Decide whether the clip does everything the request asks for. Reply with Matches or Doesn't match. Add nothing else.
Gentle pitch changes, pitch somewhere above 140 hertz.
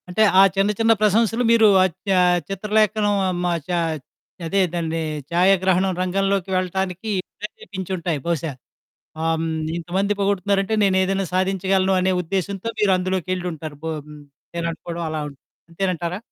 Matches